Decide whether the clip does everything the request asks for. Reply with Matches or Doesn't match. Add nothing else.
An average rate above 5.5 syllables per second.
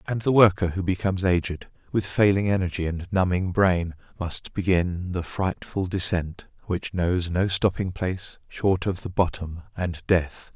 Doesn't match